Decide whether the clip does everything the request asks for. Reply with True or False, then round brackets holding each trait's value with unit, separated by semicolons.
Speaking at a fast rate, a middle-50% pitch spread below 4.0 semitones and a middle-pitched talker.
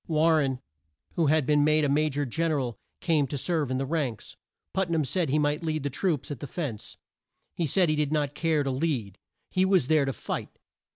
True (230 wpm; 2.9 semitones; 150 Hz)